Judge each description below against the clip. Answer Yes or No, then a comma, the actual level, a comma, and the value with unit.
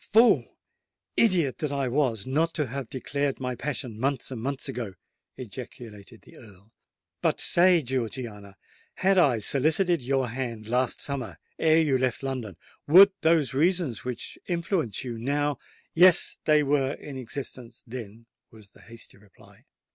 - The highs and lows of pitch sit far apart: No, average, 4.4 semitones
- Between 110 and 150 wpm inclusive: Yes, average, 140 wpm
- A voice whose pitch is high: No, low, 130 Hz